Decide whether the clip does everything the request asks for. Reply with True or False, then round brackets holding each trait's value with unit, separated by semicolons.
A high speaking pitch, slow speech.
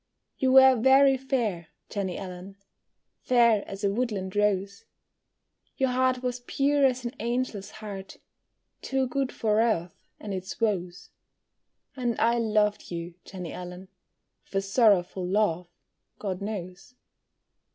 True (210 Hz; 130 wpm)